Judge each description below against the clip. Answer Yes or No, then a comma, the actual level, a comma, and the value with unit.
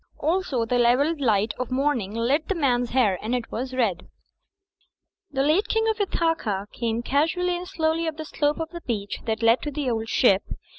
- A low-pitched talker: No, very high, 260 Hz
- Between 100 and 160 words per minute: No, average, 195 wpm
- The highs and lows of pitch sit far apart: Yes, wide, 5.8 semitones